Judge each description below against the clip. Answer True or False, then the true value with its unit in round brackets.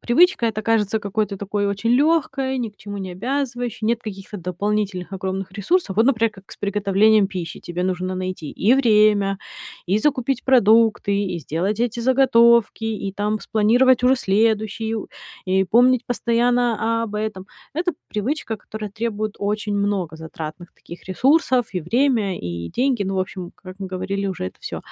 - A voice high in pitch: True (210 Hz)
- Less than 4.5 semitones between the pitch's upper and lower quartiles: True (3.6 semitones)